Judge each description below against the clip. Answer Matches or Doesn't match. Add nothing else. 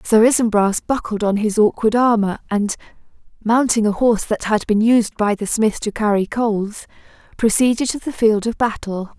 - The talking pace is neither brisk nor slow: Matches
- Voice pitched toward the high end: Matches